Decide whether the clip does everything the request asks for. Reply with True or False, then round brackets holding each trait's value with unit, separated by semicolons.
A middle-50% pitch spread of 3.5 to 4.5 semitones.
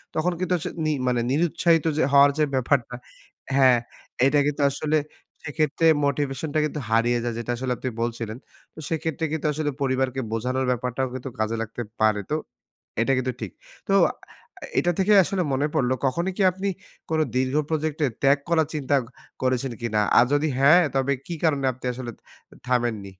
True (3.9 semitones)